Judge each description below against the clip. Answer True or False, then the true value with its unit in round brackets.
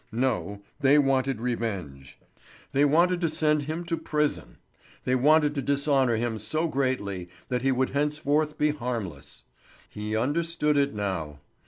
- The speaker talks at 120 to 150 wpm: True (145 wpm)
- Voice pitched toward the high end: False (135 Hz)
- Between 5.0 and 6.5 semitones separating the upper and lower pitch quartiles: True (5.3 semitones)